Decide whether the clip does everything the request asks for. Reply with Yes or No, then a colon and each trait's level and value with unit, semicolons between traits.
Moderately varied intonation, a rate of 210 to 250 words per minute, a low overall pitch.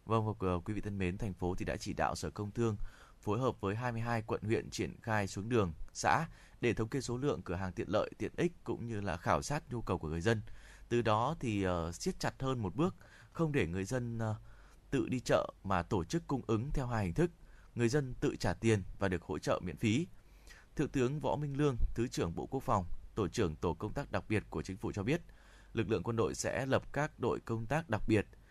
Yes: average, 4.1 semitones; average, 245 wpm; low, 110 Hz